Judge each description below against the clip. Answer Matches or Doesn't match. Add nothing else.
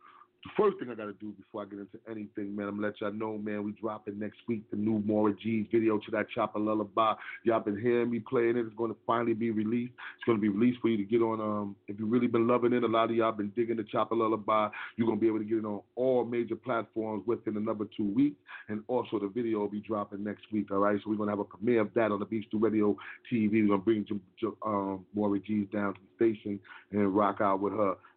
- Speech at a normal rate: Doesn't match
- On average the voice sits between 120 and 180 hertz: Doesn't match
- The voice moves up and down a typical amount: Doesn't match